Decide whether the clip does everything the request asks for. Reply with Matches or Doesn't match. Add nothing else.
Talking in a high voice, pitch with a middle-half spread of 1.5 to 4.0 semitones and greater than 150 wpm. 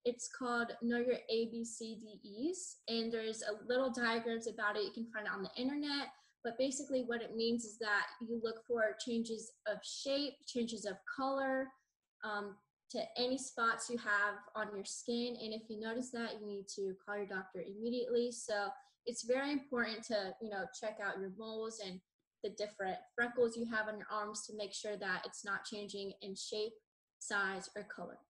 Matches